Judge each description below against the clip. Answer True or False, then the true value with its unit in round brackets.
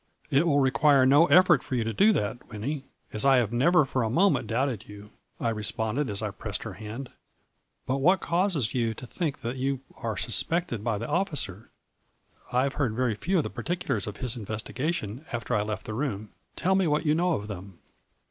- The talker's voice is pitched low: True (130 Hz)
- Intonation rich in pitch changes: True (5.7 semitones)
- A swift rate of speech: True (215 wpm)